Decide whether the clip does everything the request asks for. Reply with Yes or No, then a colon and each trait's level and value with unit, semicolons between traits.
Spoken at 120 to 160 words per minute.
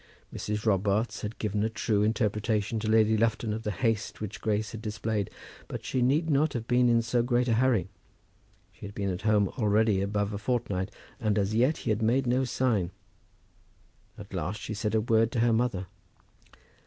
No: average, 190 wpm